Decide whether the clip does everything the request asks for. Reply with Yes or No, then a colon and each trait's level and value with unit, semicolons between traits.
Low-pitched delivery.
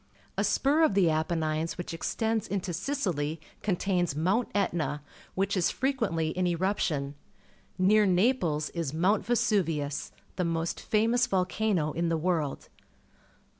No: medium, 180 Hz